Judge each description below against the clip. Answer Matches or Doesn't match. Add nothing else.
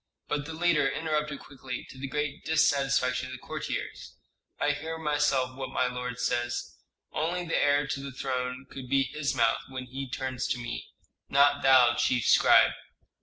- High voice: Doesn't match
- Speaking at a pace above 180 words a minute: Doesn't match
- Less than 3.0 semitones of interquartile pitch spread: Matches